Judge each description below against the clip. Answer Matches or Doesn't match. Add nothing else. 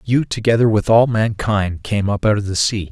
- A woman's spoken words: Doesn't match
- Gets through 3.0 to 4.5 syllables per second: Doesn't match